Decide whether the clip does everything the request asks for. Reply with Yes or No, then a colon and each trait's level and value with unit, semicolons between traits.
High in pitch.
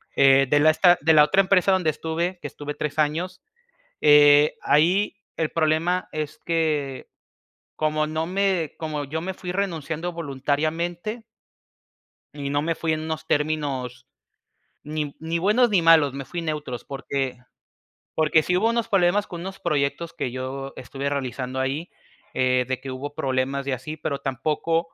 No: medium, 155 Hz